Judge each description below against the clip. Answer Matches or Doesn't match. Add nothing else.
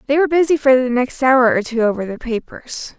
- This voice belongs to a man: Doesn't match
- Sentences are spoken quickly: Matches